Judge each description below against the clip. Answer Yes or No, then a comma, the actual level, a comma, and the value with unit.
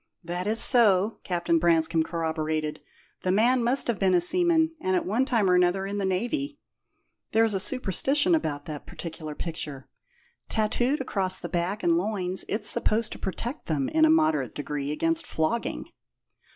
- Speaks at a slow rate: No, average, 165 wpm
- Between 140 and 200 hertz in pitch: Yes, high, 190 Hz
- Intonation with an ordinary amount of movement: No, wide, 6.3 semitones